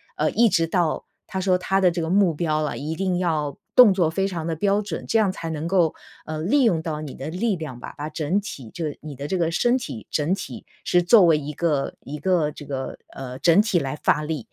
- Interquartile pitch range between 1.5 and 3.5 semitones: No, average, 4.0 semitones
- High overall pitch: No, medium, 165 Hz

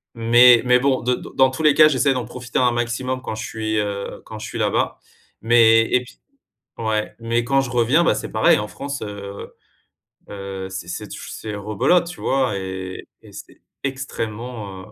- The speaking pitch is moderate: No, low, 120 Hz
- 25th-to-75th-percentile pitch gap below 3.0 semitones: No, average, 3.6 semitones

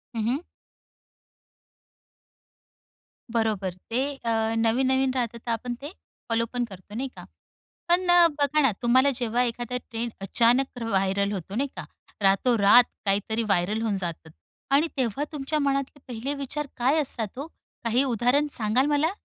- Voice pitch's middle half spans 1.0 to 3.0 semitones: No, average, 3.6 semitones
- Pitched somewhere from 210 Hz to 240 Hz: Yes, high, 235 Hz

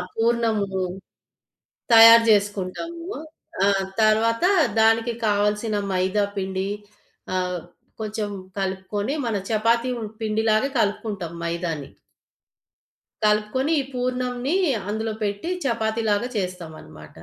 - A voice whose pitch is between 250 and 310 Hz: No, high, 215 Hz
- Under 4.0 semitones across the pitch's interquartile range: Yes, average, 2.7 semitones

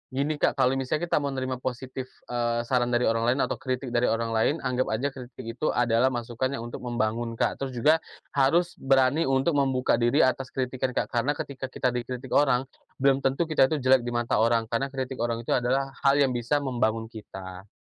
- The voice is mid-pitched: No, low, 130 Hz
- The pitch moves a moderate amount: No, narrow, 2.2 semitones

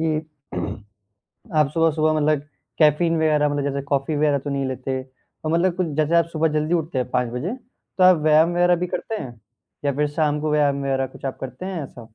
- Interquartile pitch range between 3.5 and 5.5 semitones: No, average, 2.8 semitones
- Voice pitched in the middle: Yes, medium, 150 Hz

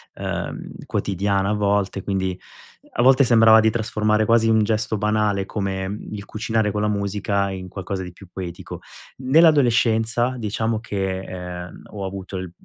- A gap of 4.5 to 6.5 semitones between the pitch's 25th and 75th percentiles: No, narrow, 2.5 semitones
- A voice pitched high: No, low, 105 Hz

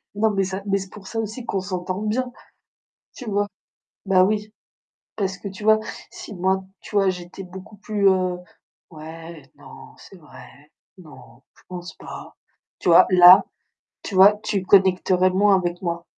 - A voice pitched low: No, high, 190 Hz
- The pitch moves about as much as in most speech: No, narrow, 2.3 semitones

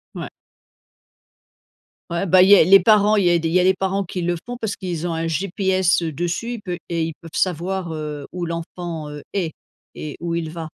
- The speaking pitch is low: No, medium, 175 Hz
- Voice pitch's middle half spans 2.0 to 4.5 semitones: Yes, narrow, 2.6 semitones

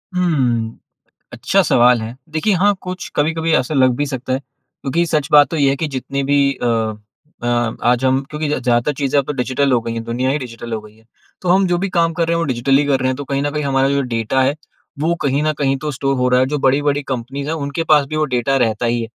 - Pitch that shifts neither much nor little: Yes, average, 3.4 semitones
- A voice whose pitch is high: No, low, 135 Hz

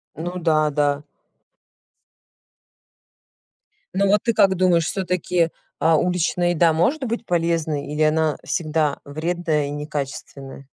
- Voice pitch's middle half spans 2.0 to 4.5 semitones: Yes, average, 2.9 semitones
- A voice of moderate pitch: Yes, medium, 165 Hz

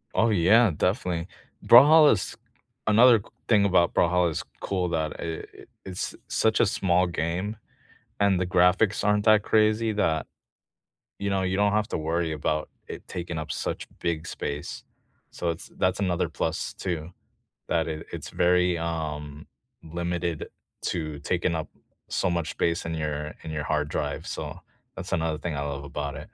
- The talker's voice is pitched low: Yes, very low, 85 Hz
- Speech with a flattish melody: No, average, 3.6 semitones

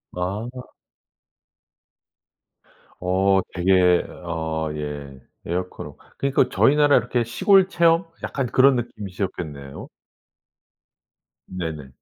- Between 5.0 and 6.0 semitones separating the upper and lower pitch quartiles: No, wide, 7.4 semitones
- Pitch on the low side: Yes, very low, 95 Hz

